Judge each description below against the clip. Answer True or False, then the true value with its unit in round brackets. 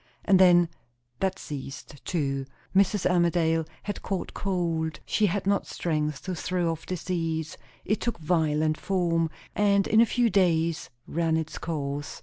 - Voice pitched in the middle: True (170 Hz)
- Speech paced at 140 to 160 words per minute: True (145 wpm)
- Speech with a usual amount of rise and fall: True (3.0 semitones)